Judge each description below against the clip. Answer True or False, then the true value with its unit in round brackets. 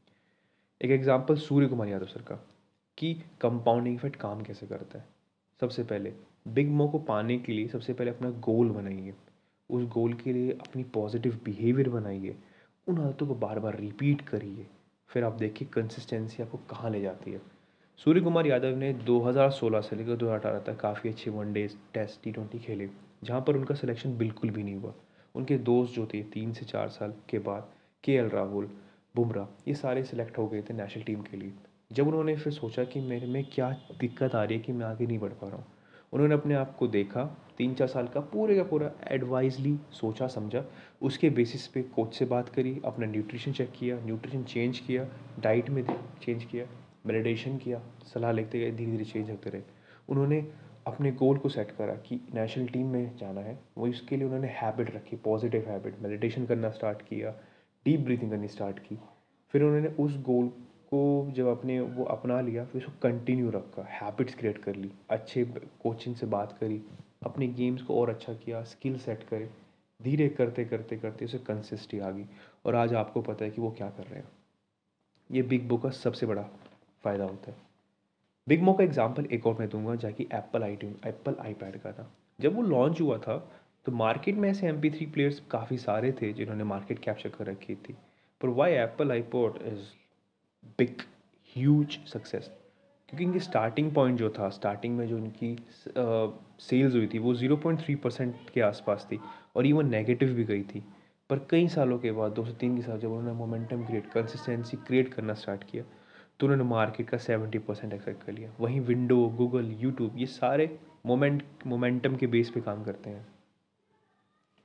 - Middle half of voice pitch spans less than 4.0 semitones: True (3.3 semitones)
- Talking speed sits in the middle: False (195 wpm)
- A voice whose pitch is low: True (120 Hz)